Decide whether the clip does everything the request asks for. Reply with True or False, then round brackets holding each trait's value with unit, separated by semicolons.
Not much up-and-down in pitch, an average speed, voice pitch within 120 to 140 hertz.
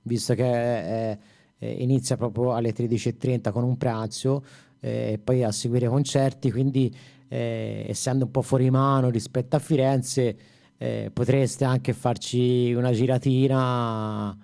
True (1.9 semitones; 135 wpm; 125 Hz)